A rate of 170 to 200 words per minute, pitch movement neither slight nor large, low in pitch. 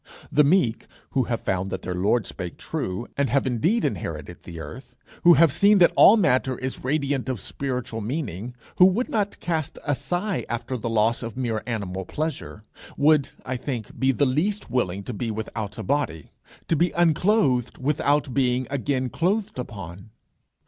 No: average, 175 wpm; wide, 5.9 semitones; low, 130 Hz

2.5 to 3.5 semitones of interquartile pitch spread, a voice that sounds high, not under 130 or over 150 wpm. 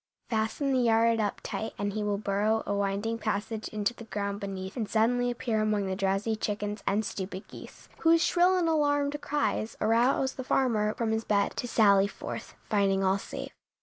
No: average, 3.0 semitones; high, 215 Hz; average, 185 wpm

